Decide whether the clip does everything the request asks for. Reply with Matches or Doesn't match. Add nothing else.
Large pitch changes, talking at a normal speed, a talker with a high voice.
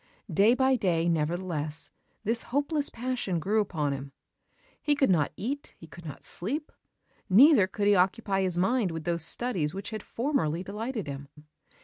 Matches